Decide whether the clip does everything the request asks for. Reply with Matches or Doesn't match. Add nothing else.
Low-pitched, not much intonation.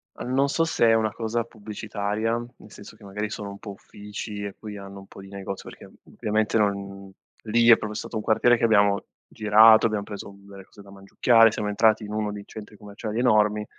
Matches